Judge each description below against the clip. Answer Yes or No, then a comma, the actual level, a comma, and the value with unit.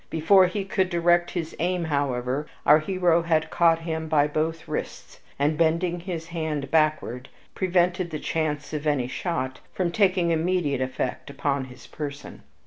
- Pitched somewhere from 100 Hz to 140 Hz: No, medium, 160 Hz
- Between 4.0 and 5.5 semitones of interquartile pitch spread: No, average, 3.1 semitones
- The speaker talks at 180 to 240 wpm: No, average, 155 wpm